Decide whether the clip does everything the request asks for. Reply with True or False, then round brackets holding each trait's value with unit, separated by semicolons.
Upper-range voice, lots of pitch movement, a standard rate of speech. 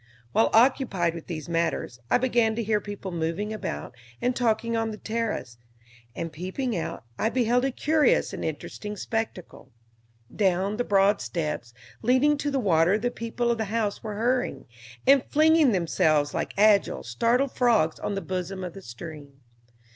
True (210 Hz; 5.9 semitones; 165 wpm)